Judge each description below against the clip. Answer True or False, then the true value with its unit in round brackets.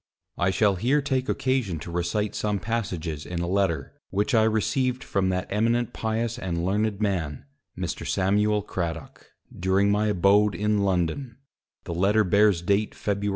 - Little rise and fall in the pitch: False (3.2 semitones)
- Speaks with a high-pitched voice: False (100 Hz)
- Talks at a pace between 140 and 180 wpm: True (155 wpm)